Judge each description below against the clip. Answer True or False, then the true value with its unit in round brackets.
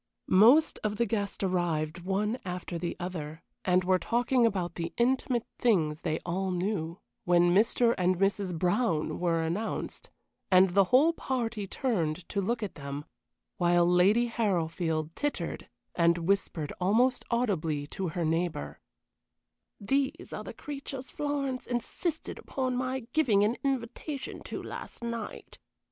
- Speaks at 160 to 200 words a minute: False (140 wpm)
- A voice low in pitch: False (195 Hz)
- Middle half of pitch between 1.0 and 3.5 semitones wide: False (5.6 semitones)